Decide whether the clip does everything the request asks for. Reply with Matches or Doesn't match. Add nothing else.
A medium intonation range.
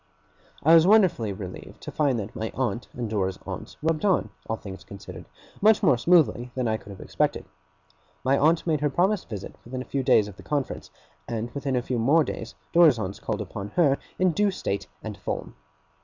Doesn't match